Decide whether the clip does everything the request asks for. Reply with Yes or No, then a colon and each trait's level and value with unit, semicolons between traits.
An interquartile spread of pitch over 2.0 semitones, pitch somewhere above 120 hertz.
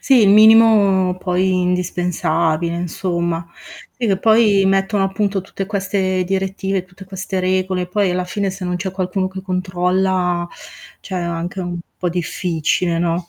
No: narrow, 1.5 semitones; medium, 185 Hz